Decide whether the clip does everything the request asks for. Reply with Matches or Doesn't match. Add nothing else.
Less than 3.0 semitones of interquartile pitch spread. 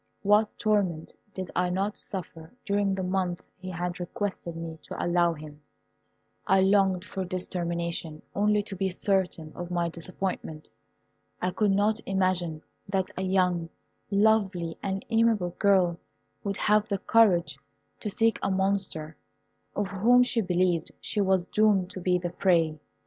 Matches